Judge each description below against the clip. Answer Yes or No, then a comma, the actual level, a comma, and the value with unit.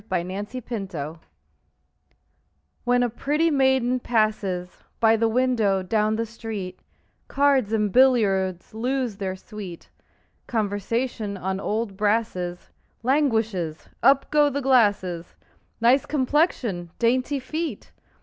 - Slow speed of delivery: Yes, slow, 115 wpm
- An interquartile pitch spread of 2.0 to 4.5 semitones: No, average, 4.9 semitones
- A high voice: Yes, high, 225 Hz